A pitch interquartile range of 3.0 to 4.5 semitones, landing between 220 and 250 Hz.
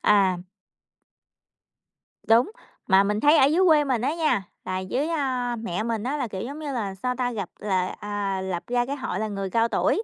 No: average, 5.3 semitones; high, 230 Hz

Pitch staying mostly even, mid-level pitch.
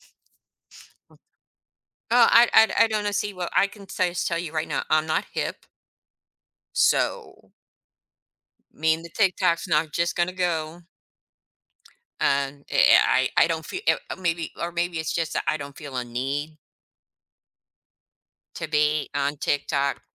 No: average, 3.3 semitones; medium, 165 Hz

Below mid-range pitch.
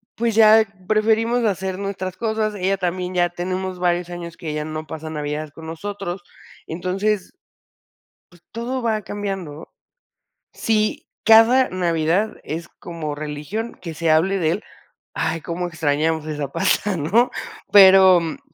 No: medium, 180 Hz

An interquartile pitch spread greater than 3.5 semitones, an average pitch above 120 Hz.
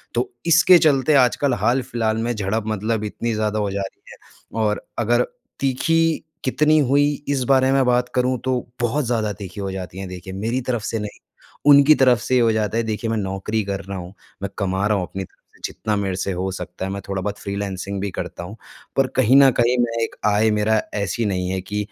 No: average, 4.1 semitones; low, 110 Hz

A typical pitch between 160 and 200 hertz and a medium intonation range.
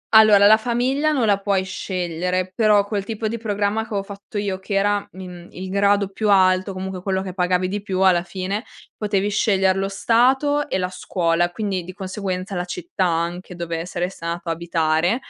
No: high, 190 Hz; narrow, 2.3 semitones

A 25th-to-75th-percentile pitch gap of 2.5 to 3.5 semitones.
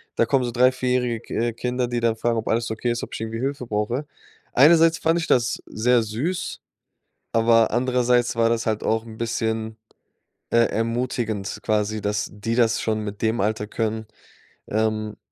No: narrow, 2.0 semitones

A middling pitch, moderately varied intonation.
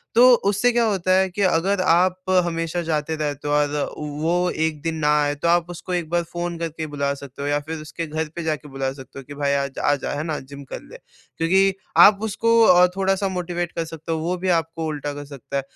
Yes: medium, 165 Hz; average, 3.5 semitones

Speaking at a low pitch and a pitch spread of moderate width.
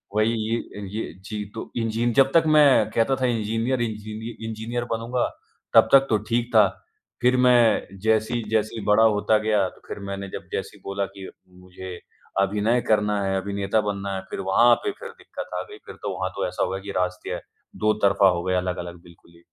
Yes: low, 110 Hz; average, 3.0 semitones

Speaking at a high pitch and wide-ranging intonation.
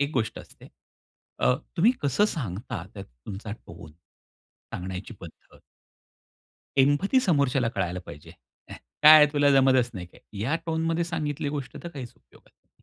No: low, 135 Hz; wide, 7.6 semitones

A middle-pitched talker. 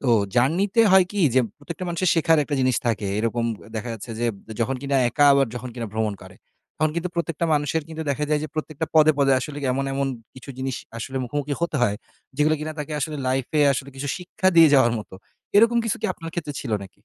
Yes: medium, 145 Hz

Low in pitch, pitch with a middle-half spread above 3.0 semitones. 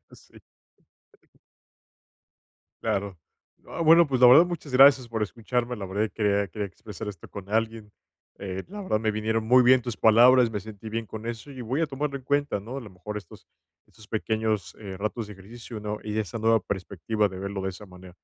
Yes: low, 110 Hz; average, 3.4 semitones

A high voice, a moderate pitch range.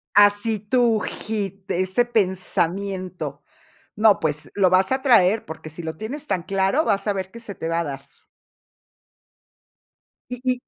Yes: high, 195 Hz; average, 3.7 semitones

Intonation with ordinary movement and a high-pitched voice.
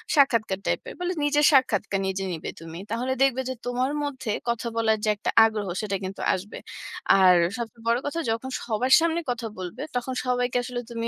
Yes: average, 3.7 semitones; high, 235 Hz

